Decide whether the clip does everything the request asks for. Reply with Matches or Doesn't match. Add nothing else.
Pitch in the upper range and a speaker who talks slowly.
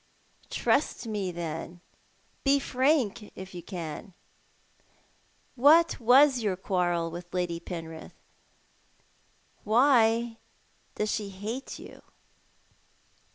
Matches